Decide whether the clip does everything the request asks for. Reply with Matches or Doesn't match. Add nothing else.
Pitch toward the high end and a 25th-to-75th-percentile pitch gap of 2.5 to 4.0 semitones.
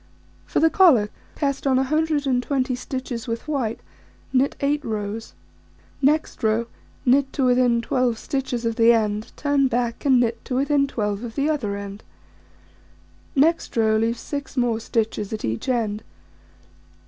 Matches